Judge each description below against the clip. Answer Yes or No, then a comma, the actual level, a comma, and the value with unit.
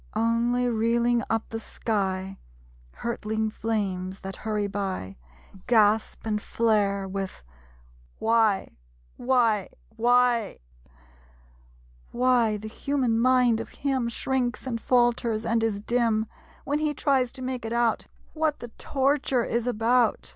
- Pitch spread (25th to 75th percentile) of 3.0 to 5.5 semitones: No, narrow, 2.5 semitones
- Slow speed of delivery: Yes, slow, 120 wpm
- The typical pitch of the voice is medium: No, high, 230 Hz